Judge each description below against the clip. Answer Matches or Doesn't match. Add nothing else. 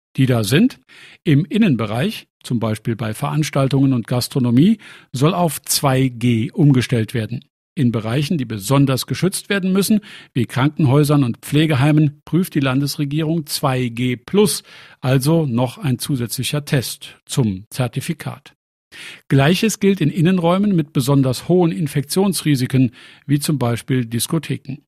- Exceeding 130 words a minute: Doesn't match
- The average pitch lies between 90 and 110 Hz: Doesn't match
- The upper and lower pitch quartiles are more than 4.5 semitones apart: Doesn't match